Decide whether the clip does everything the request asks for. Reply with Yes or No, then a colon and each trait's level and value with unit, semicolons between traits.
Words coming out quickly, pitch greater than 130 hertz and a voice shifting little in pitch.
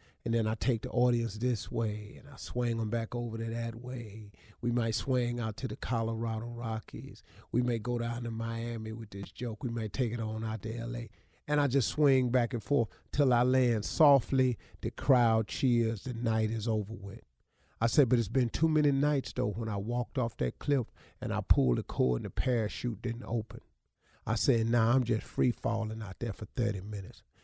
No: fast, 215 wpm; low, 115 Hz; narrow, 2.0 semitones